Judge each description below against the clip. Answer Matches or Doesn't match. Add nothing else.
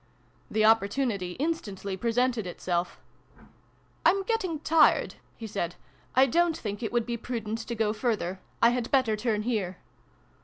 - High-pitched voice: Matches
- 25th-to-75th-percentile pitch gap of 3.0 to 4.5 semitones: Matches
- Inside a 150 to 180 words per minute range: Matches